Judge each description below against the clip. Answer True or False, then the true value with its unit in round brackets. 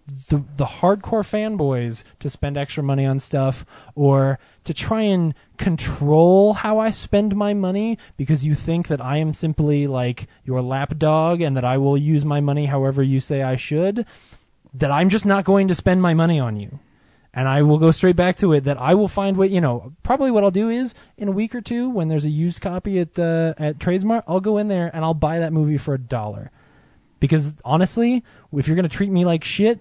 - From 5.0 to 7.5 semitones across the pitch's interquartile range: True (5.5 semitones)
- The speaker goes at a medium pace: False (220 wpm)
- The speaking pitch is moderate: True (155 Hz)